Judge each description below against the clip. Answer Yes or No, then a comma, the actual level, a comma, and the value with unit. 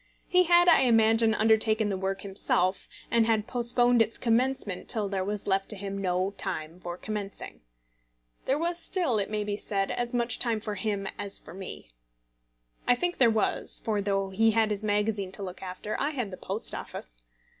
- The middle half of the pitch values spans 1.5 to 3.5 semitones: Yes, average, 3.2 semitones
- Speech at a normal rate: Yes, average, 190 wpm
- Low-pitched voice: No, high, 215 Hz